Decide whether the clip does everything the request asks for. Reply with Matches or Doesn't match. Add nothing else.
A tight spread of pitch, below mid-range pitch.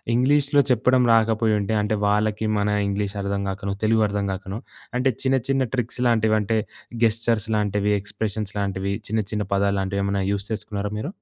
Matches